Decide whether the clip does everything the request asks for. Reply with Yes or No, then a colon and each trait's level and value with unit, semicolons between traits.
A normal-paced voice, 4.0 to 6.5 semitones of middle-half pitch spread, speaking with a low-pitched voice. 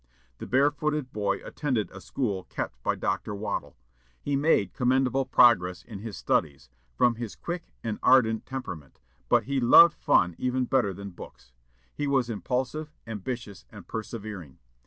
Yes: average, 150 wpm; average, 5.1 semitones; low, 115 Hz